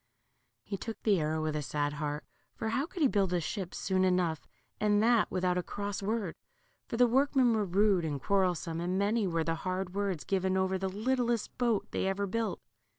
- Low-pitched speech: No, high, 195 Hz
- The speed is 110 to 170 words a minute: No, fast, 205 wpm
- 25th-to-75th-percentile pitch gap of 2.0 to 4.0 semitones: Yes, average, 3.7 semitones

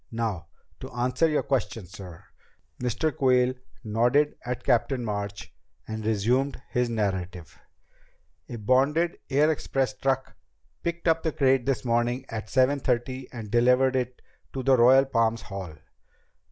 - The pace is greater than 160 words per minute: No, average, 140 wpm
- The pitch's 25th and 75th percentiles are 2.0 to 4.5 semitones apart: Yes, average, 3.2 semitones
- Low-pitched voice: Yes, low, 125 Hz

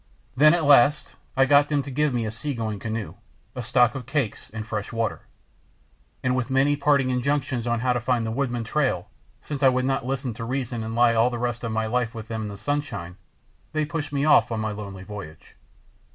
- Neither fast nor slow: No, fast, 220 wpm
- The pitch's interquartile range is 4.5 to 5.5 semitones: No, average, 3.8 semitones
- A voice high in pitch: No, low, 125 Hz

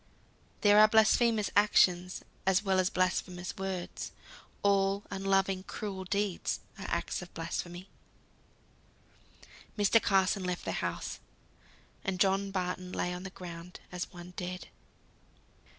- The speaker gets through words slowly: Yes, slow, 120 wpm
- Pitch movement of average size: No, narrow, 1.8 semitones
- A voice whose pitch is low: No, high, 190 Hz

